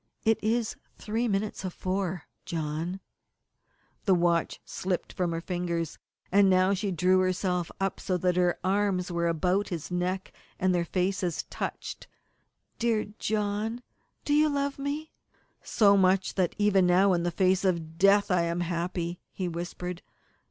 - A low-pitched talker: No, medium, 185 Hz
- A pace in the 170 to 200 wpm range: No, average, 150 wpm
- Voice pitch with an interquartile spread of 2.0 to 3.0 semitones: Yes, narrow, 2.4 semitones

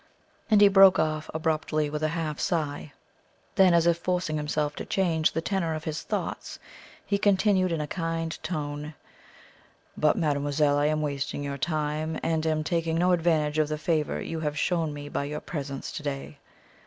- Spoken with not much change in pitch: Yes, narrow, 2.1 semitones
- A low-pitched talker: No, medium, 155 Hz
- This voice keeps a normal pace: Yes, average, 180 wpm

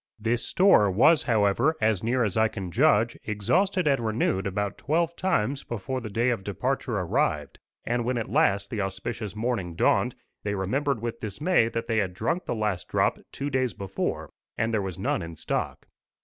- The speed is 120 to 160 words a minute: No, average, 185 wpm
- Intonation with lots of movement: No, average, 4.3 semitones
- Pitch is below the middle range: Yes, low, 110 Hz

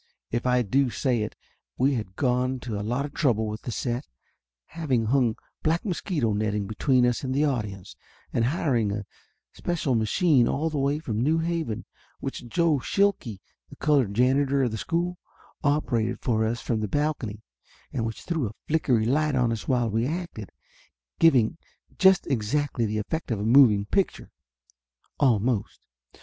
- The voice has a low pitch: Yes, low, 125 Hz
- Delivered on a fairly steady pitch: No, average, 5.0 semitones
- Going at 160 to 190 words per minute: Yes, average, 165 wpm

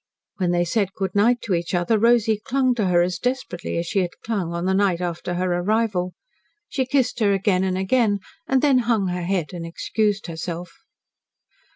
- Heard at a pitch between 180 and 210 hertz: Yes, high, 190 Hz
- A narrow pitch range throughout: No, average, 4.4 semitones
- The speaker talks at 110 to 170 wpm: No, average, 195 wpm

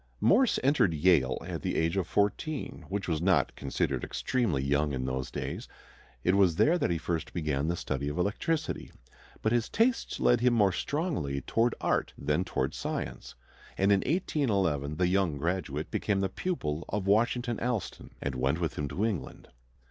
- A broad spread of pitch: Yes, wide, 7.7 semitones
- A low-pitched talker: Yes, very low, 95 Hz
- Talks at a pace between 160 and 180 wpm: Yes, average, 175 wpm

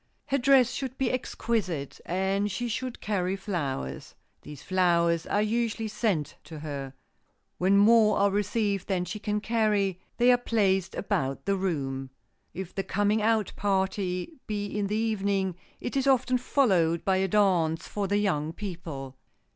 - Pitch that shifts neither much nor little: Yes, average, 3.6 semitones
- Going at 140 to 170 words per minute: Yes, average, 155 wpm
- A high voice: Yes, high, 200 Hz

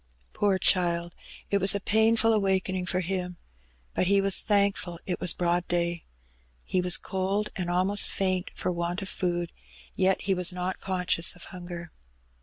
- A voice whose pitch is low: No, medium, 185 Hz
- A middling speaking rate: Yes, average, 170 wpm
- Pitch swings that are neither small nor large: No, narrow, 1.8 semitones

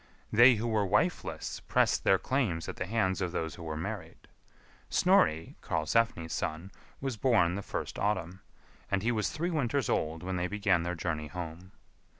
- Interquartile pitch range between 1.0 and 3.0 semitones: No, average, 5.1 semitones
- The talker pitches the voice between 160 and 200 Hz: No, very low, 95 Hz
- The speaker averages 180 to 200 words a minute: No, average, 170 wpm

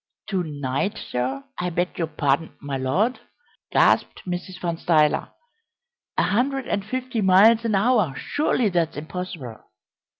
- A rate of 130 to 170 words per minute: Yes, slow, 135 wpm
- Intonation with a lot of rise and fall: Yes, wide, 6.2 semitones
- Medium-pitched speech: Yes, medium, 180 Hz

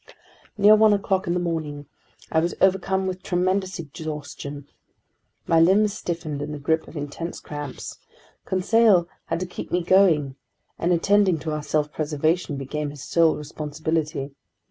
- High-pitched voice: No, medium, 165 Hz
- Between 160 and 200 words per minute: No, average, 150 wpm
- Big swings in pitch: No, average, 3.8 semitones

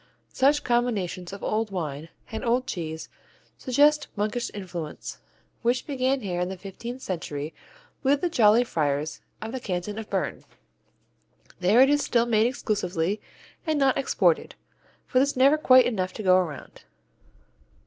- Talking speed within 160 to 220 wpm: No, average, 150 wpm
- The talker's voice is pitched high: Yes, high, 220 Hz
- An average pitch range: No, wide, 6.1 semitones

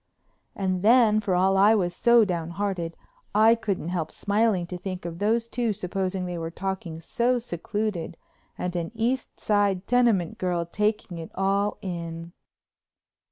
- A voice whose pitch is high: Yes, high, 195 Hz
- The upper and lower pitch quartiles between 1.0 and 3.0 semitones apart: No, average, 3.6 semitones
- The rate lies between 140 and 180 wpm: Yes, average, 150 wpm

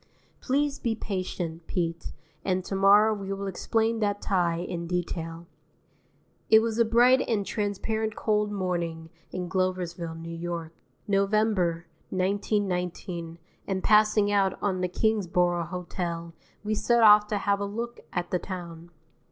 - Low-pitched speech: No, high, 190 Hz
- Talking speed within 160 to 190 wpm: No, average, 140 wpm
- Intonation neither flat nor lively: Yes, average, 3.4 semitones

